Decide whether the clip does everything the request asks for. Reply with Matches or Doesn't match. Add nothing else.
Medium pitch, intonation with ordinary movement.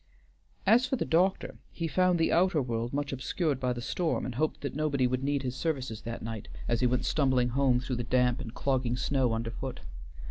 Doesn't match